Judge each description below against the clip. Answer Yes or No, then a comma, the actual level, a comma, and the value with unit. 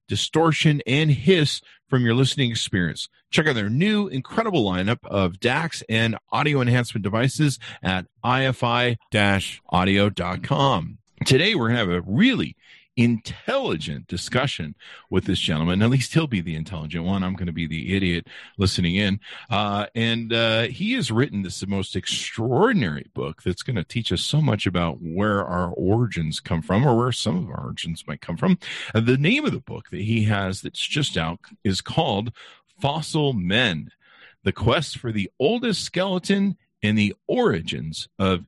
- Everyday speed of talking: Yes, average, 170 wpm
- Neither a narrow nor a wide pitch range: No, wide, 5.8 semitones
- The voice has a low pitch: Yes, low, 115 Hz